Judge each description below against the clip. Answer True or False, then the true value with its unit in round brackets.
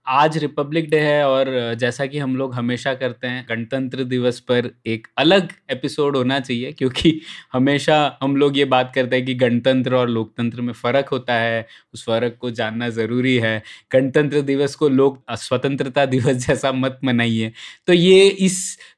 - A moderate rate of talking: True (170 wpm)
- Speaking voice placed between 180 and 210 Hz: False (130 Hz)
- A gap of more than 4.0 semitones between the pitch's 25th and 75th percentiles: False (2.7 semitones)